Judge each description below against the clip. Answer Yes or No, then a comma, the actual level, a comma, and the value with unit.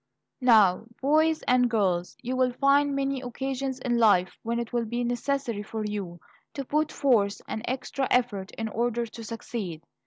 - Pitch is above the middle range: Yes, high, 240 Hz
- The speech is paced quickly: No, average, 165 wpm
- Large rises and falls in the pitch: No, average, 3.6 semitones